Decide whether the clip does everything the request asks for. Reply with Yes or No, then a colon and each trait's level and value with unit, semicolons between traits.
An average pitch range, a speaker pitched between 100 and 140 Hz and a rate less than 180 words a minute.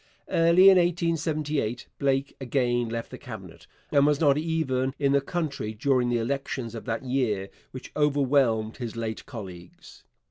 Yes: average, 4.1 semitones; low, 135 Hz; average, 155 wpm